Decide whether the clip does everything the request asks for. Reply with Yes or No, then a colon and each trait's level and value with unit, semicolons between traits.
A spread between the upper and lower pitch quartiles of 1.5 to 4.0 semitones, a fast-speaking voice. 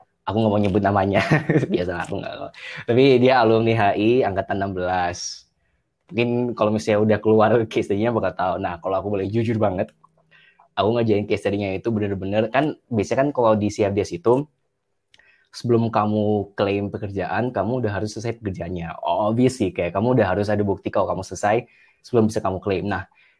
Yes: narrow, 2.6 semitones; fast, 170 wpm